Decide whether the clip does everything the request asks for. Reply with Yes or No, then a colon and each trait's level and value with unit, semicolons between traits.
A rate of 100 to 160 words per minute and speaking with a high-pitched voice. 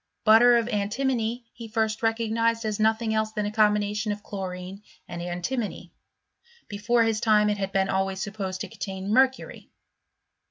Yes: average, 155 wpm; high, 215 Hz